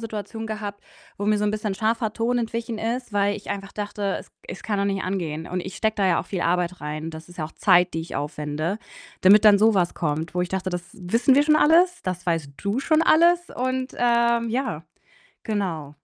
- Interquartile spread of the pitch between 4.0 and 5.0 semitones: Yes, average, 4.5 semitones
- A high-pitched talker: Yes, high, 205 Hz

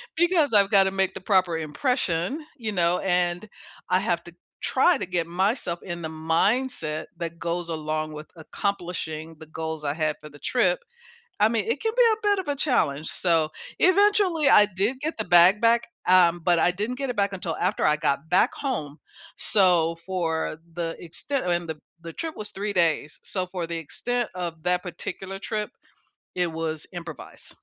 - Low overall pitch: No, medium, 180 Hz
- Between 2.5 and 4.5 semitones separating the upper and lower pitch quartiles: No, average, 4.9 semitones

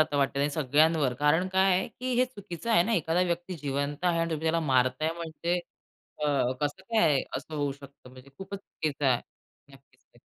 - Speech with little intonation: No, average, 4.0 semitones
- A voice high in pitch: No, medium, 160 Hz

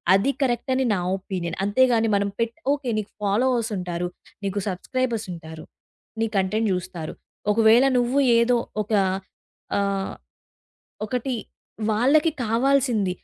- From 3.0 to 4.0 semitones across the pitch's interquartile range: No, average, 4.4 semitones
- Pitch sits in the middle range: No, high, 225 Hz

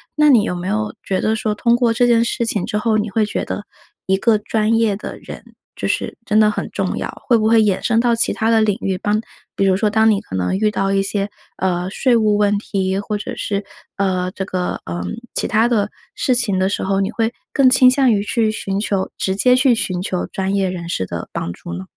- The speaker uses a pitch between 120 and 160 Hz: No, high, 210 Hz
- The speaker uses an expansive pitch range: No, average, 2.9 semitones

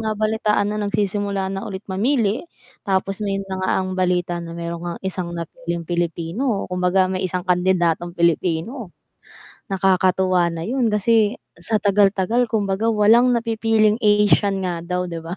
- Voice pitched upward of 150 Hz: Yes, high, 190 Hz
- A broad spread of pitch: No, average, 3.1 semitones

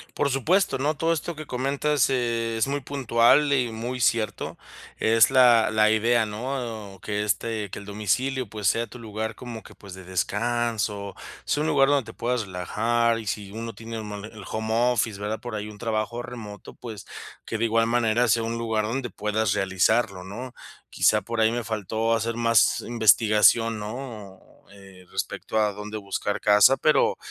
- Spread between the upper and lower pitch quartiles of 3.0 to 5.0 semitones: No, narrow, 2.4 semitones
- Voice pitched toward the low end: Yes, low, 115 Hz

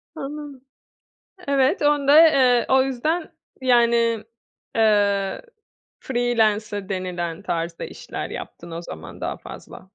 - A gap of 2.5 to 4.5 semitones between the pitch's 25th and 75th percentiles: No, average, 5.3 semitones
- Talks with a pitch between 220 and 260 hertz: Yes, high, 235 Hz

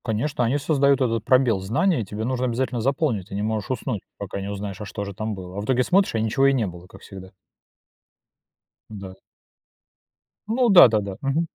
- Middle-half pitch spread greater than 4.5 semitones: Yes, average, 5.1 semitones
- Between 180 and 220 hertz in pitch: No, low, 110 Hz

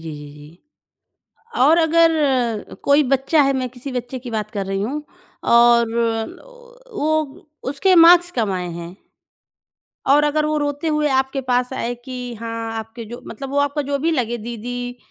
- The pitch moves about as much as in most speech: Yes, average, 4.2 semitones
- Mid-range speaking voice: No, very high, 260 Hz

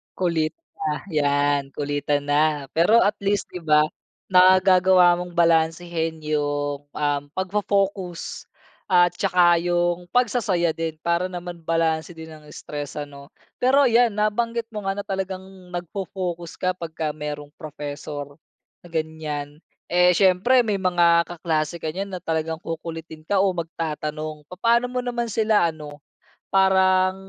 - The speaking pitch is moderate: Yes, medium, 170 Hz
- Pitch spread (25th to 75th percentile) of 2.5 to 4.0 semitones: Yes, average, 3.5 semitones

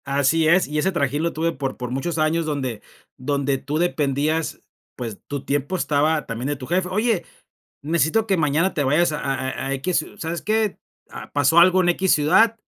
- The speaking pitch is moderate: Yes, medium, 155 Hz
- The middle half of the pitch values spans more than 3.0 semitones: Yes, average, 3.7 semitones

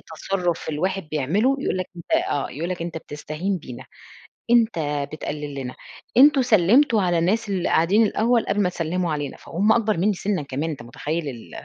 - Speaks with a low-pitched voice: No, medium, 175 Hz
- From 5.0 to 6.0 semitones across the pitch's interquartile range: Yes, wide, 5.5 semitones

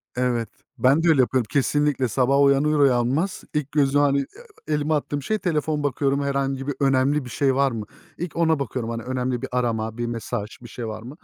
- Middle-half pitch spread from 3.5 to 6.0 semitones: No, average, 2.9 semitones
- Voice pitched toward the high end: No, low, 135 Hz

